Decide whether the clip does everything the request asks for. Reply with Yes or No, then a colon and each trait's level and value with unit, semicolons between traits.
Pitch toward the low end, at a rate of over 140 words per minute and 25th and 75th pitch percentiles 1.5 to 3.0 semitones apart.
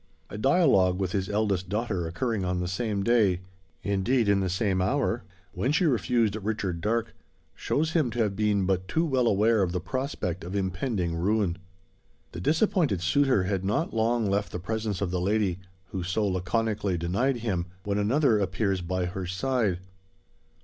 No: low, 100 Hz; average, 170 wpm; average, 3.9 semitones